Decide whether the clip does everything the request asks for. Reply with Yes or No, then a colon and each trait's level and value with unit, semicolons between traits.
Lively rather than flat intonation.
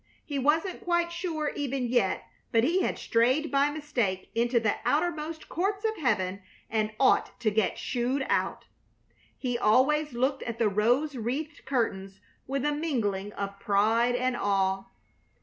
Yes: wide, 5.7 semitones